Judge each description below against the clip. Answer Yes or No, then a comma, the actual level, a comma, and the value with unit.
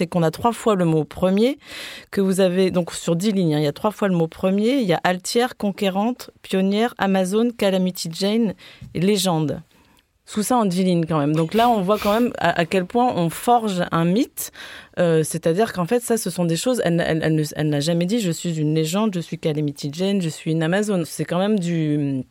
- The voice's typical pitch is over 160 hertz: Yes, medium, 185 Hz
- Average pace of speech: No, fast, 240 wpm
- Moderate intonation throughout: Yes, average, 4.5 semitones